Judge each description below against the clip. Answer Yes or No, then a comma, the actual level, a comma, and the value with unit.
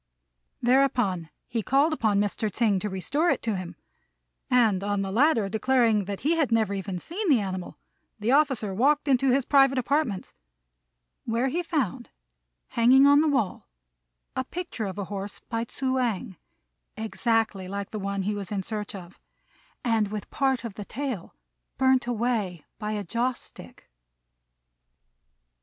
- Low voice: No, high, 225 Hz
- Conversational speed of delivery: Yes, average, 155 wpm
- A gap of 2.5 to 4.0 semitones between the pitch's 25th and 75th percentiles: No, average, 4.9 semitones